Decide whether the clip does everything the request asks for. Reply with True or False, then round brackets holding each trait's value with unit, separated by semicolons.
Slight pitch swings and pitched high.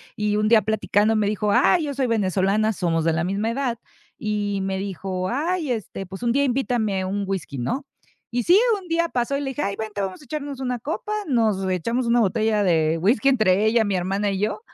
False (4.3 semitones; 215 Hz)